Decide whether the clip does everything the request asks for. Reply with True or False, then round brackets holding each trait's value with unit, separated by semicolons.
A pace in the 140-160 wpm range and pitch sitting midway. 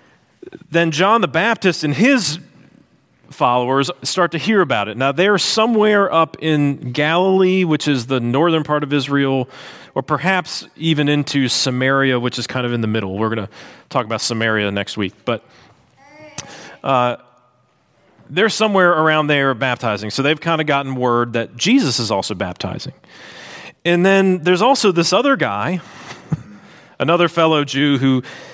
True (155 wpm; 150 Hz)